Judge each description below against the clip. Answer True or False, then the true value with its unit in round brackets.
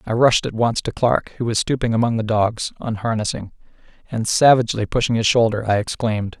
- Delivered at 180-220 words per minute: True (190 wpm)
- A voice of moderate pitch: False (115 Hz)